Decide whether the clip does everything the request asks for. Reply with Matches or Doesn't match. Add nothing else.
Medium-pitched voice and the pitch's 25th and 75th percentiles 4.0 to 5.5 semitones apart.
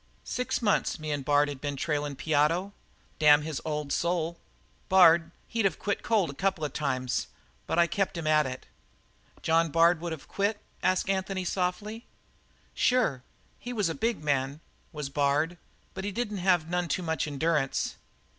Matches